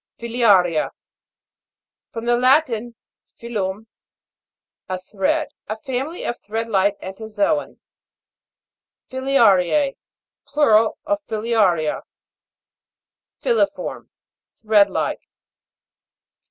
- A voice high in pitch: Yes, high, 225 Hz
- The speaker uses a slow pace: Yes, slow, 75 wpm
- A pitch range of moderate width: Yes, average, 4.5 semitones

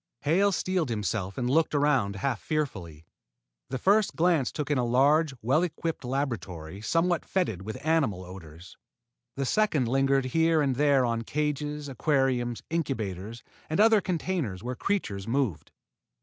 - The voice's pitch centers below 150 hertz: Yes, low, 135 Hz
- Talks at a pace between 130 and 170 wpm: Yes, average, 150 wpm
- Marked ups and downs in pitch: Yes, wide, 6.1 semitones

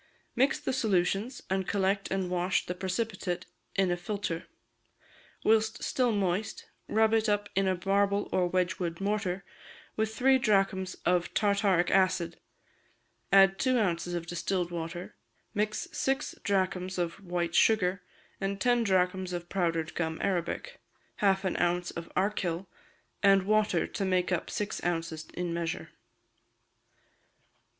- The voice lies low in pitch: No, high, 190 Hz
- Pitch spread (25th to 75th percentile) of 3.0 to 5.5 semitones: No, narrow, 2.6 semitones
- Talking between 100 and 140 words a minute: Yes, slow, 135 wpm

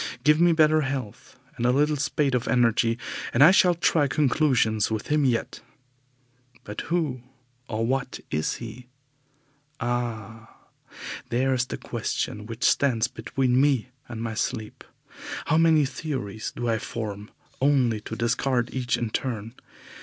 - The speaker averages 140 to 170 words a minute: Yes, average, 145 wpm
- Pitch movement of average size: Yes, average, 3.9 semitones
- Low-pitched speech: Yes, low, 125 Hz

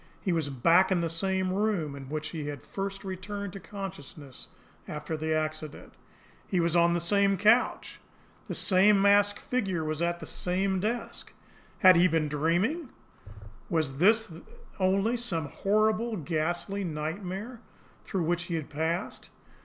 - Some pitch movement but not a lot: Yes, average, 4.0 semitones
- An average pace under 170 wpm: Yes, average, 155 wpm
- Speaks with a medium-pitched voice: Yes, medium, 180 Hz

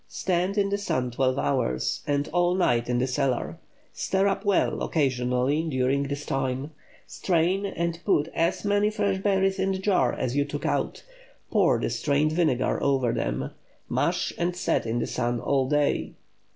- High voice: No, medium, 145 Hz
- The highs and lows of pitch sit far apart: Yes, wide, 6.6 semitones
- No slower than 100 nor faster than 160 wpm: No, average, 170 wpm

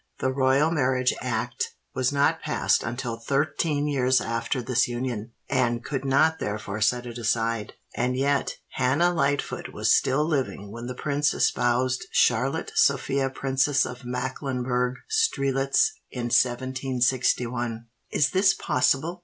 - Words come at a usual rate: No, slow, 130 wpm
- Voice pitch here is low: Yes, low, 130 Hz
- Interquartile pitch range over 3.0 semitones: No, narrow, 2.5 semitones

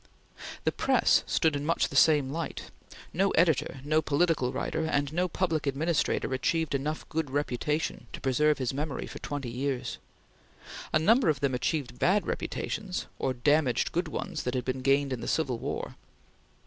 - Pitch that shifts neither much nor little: Yes, average, 3.4 semitones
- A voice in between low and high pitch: Yes, medium, 145 Hz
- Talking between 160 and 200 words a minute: Yes, average, 170 wpm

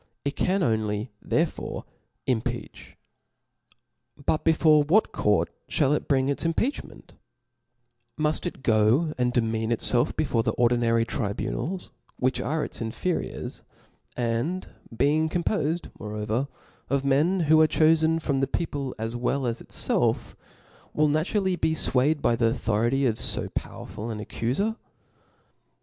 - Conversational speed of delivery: No, slow, 130 wpm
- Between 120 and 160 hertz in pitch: Yes, low, 135 Hz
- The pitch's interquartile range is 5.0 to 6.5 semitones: Yes, wide, 5.4 semitones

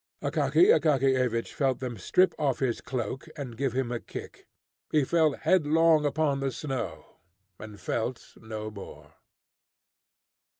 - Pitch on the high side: No, low, 135 Hz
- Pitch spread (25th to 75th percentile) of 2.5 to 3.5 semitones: No, average, 4.2 semitones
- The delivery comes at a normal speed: No, slow, 130 wpm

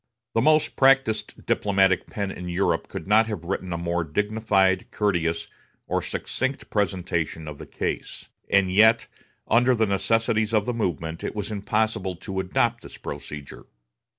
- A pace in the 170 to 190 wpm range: No, average, 150 wpm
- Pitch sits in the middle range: No, low, 100 Hz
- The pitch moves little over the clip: No, average, 3.9 semitones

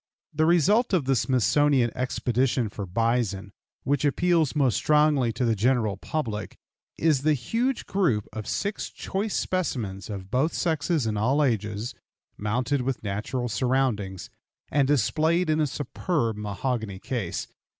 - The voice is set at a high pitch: No, low, 130 Hz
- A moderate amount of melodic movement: No, wide, 6.0 semitones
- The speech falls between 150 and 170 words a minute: No, average, 140 wpm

